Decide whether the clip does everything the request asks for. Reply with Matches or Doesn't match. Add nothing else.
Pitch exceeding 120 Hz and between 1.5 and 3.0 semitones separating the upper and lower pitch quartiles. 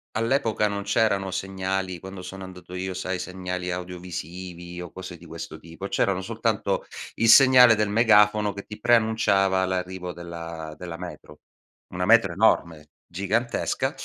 Doesn't match